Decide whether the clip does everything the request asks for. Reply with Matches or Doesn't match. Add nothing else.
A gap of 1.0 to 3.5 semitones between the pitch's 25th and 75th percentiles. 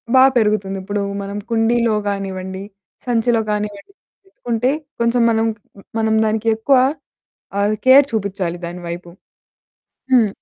Matches